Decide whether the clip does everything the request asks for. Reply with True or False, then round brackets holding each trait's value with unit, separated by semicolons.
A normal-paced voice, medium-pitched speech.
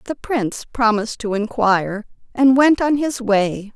False (160 wpm; 235 Hz)